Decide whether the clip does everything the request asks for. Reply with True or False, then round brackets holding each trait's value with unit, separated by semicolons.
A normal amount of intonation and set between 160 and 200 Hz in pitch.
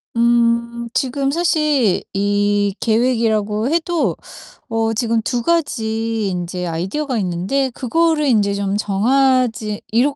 False (4.6 semitones; 230 Hz)